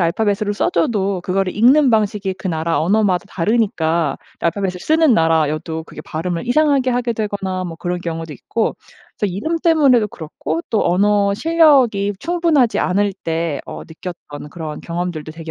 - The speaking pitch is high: Yes, high, 195 Hz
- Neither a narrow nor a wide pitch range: No, wide, 5.8 semitones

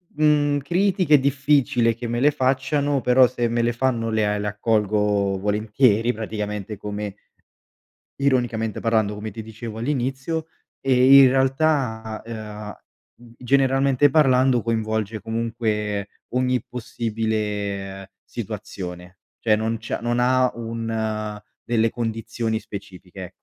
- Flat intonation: No, average, 3.5 semitones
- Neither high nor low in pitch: No, low, 115 Hz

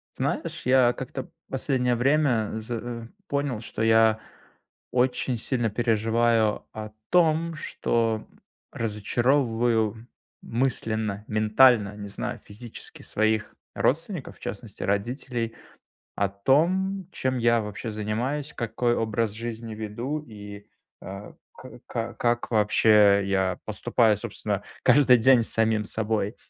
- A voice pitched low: Yes, low, 115 Hz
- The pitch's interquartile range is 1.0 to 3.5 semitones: Yes, average, 2.7 semitones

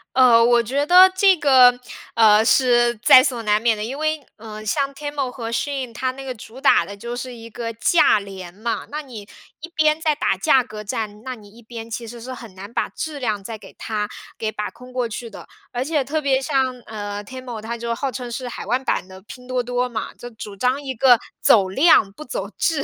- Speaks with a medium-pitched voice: No, high, 240 Hz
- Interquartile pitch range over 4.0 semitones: No, average, 3.4 semitones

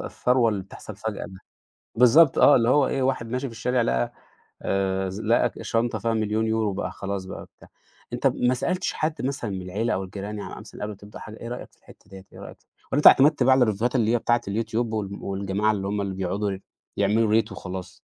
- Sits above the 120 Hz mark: No, low, 110 Hz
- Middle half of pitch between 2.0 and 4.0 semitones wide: Yes, average, 3.7 semitones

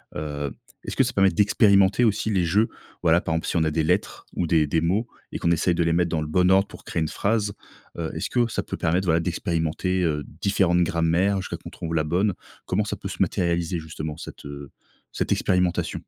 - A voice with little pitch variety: No, average, 3.1 semitones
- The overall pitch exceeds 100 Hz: No, very low, 85 Hz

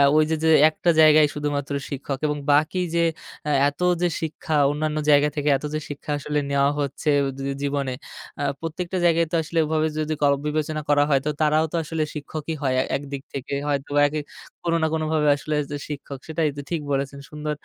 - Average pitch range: No, narrow, 1.6 semitones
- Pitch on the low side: No, medium, 150 Hz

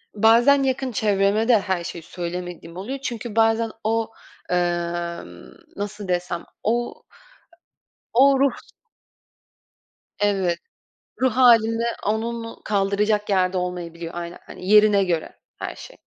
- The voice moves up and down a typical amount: Yes, average, 4.0 semitones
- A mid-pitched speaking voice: No, high, 210 Hz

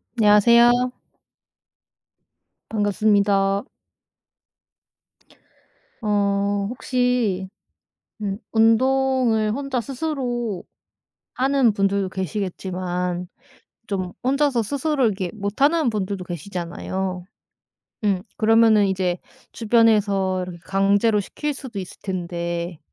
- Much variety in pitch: No, average, 4.1 semitones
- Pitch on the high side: Yes, high, 205 Hz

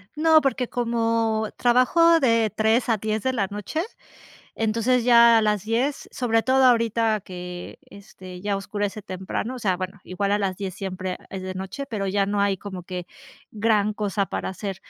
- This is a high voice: Yes, high, 215 Hz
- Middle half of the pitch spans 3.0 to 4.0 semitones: Yes, average, 3.3 semitones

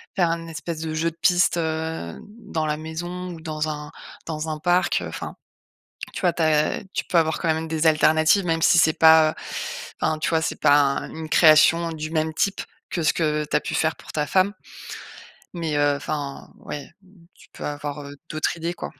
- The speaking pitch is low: No, medium, 160 Hz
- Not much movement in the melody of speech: Yes, narrow, 1.5 semitones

